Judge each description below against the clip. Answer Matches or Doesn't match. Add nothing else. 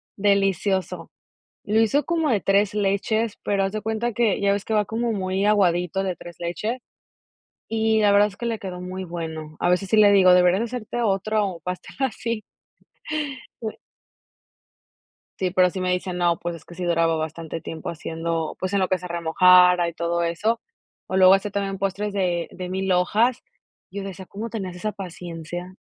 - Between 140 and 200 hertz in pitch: Matches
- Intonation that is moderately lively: Matches